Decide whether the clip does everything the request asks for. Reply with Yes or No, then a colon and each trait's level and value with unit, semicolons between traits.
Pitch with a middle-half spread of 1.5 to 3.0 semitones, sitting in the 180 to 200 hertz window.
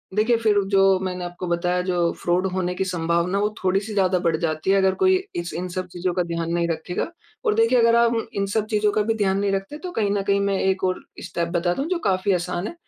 Yes: average, 2.7 semitones; high, 190 Hz